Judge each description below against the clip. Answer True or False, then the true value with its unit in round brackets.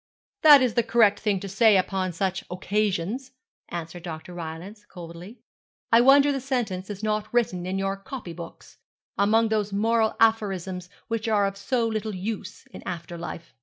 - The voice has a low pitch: False (205 Hz)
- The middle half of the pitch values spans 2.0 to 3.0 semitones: False (3.6 semitones)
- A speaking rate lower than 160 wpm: False (165 wpm)